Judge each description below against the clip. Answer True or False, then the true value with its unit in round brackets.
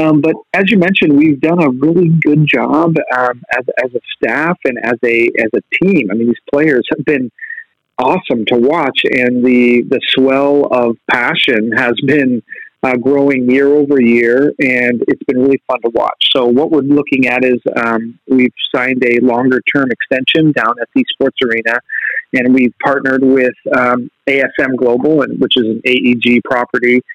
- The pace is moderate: True (180 wpm)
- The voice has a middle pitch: False (130 Hz)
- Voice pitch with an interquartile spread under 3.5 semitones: True (2.9 semitones)